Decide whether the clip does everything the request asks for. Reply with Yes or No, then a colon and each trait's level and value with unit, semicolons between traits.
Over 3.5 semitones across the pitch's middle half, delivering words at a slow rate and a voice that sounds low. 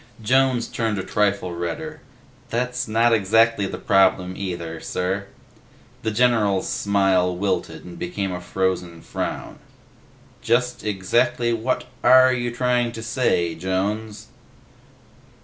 Yes: average, 4.2 semitones; slow, 115 wpm; low, 105 Hz